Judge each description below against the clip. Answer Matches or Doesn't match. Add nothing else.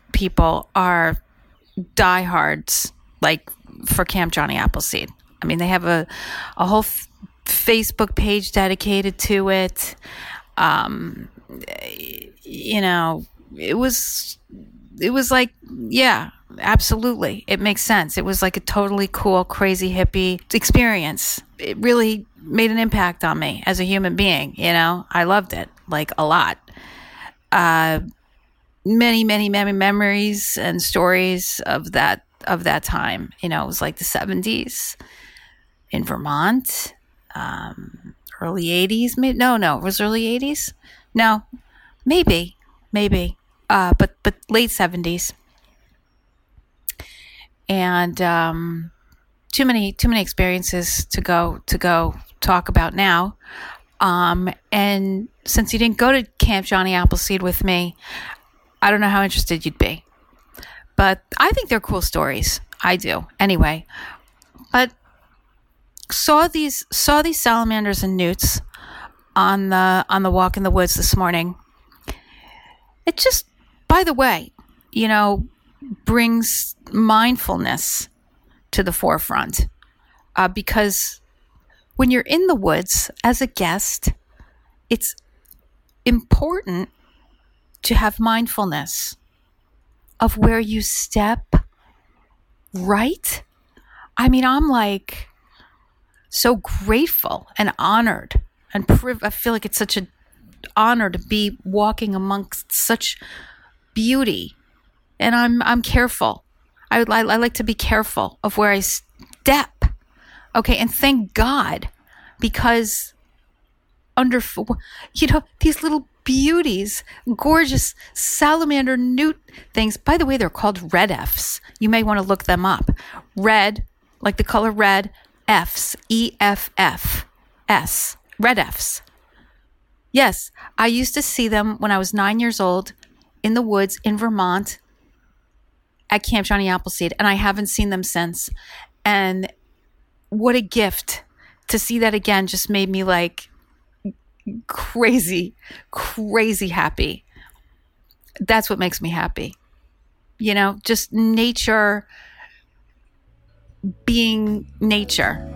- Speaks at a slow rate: Matches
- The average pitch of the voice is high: Matches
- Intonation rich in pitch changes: Doesn't match